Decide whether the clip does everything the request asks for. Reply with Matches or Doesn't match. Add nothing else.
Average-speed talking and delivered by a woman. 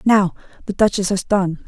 Matches